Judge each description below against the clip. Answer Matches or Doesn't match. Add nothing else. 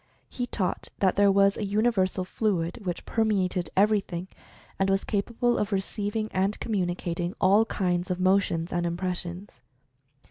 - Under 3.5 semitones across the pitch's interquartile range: Matches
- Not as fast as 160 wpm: Matches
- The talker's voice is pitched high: Matches